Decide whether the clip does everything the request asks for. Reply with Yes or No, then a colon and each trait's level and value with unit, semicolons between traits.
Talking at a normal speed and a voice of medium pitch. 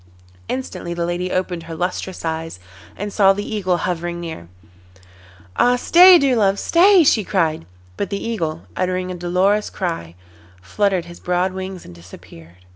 Yes: average, 155 wpm; medium, 180 Hz